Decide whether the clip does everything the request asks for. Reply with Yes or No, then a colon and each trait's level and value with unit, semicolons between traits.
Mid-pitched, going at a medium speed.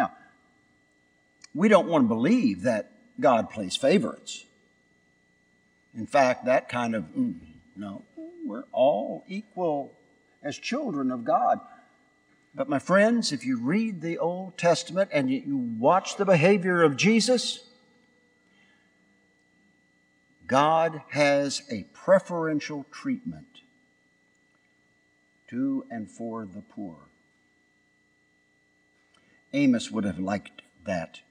No: medium, 165 Hz; slow, 105 wpm